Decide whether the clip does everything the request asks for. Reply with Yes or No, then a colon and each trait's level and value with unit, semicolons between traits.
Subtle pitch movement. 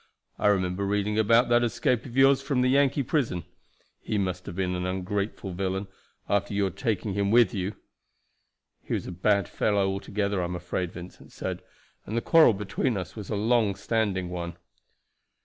No: average, 3.7 semitones